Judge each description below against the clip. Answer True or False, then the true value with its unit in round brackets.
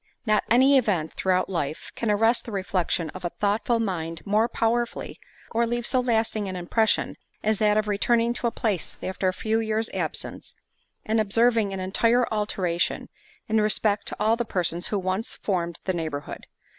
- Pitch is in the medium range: False (210 Hz)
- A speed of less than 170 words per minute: False (175 wpm)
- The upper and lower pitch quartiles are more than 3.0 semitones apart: True (3.5 semitones)